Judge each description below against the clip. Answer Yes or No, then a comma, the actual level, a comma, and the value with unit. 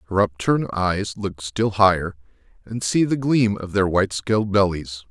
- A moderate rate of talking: Yes, average, 175 wpm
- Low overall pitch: Yes, low, 100 Hz